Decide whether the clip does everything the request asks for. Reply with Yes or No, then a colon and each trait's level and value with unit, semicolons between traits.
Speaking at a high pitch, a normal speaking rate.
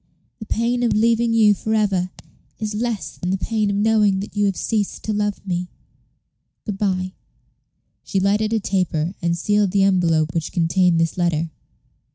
Yes: high, 200 Hz; average, 175 wpm